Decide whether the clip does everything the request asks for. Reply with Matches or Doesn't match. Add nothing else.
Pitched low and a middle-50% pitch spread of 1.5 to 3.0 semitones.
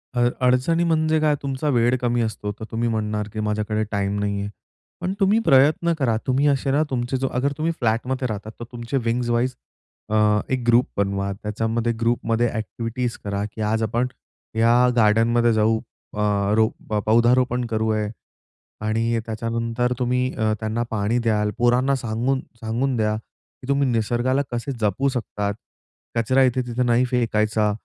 Matches